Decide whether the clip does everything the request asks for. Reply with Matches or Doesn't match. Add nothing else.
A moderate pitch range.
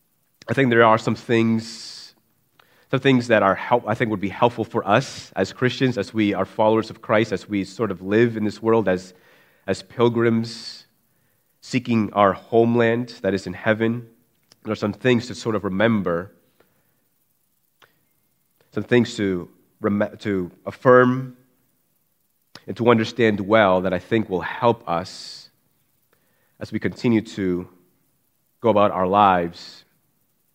Matches